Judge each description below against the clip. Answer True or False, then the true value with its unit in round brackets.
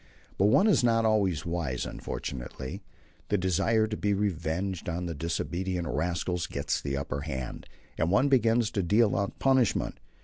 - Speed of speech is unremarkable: True (160 wpm)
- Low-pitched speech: True (90 Hz)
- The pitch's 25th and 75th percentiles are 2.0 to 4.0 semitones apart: False (4.8 semitones)